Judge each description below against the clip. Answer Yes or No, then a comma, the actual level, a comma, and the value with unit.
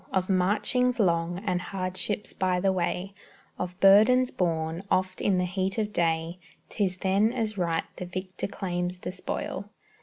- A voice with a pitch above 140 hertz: Yes, medium, 185 Hz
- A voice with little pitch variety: Yes, narrow, 1.9 semitones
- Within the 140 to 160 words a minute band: Yes, average, 155 wpm